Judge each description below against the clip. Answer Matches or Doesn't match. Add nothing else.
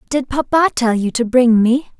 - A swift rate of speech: Matches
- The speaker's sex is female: Matches